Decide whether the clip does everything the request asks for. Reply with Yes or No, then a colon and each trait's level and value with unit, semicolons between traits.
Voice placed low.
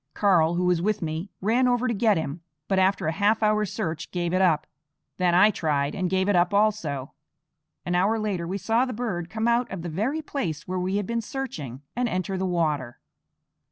No: medium, 185 Hz